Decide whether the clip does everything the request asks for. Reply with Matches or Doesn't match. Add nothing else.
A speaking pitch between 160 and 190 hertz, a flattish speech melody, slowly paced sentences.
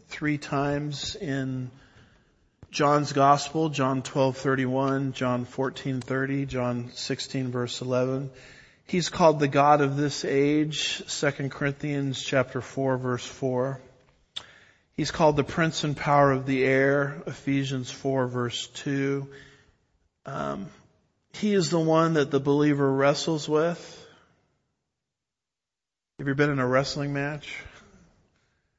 Doesn't match